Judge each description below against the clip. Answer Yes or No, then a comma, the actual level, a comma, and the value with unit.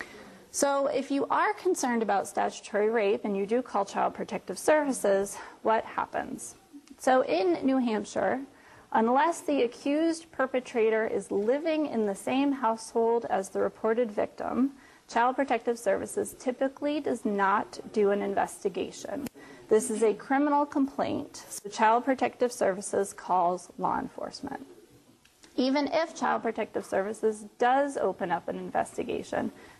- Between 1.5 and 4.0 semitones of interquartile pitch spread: No, average, 4.5 semitones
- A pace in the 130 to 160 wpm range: Yes, slow, 135 wpm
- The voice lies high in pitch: Yes, high, 245 Hz